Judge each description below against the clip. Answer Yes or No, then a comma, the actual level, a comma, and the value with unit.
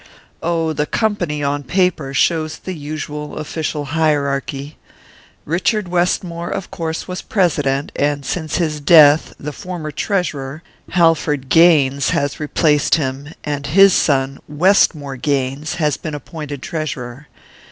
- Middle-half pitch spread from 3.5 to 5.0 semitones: No, average, 2.9 semitones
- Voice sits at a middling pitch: Yes, medium, 150 Hz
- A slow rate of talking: Yes, slow, 125 wpm